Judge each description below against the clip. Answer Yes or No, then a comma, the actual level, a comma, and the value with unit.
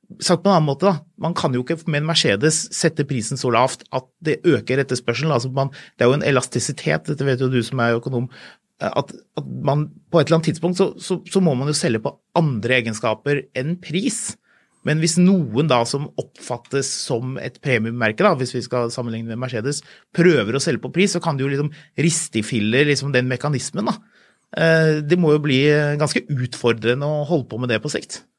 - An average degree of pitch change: Yes, average, 4.7 semitones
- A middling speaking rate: Yes, average, 190 wpm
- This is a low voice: No, medium, 145 Hz